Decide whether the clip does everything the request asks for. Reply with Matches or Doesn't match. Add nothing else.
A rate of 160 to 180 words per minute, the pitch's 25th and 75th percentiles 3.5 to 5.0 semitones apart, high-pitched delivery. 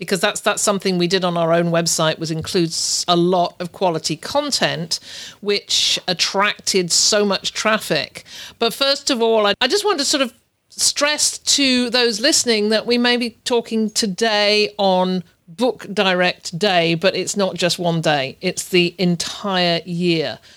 Matches